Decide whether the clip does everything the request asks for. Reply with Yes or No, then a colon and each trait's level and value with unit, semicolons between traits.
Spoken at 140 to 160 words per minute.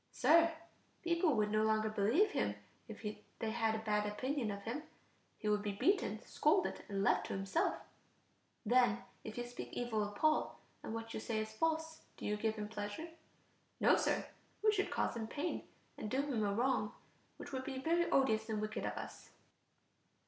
No: average, 185 wpm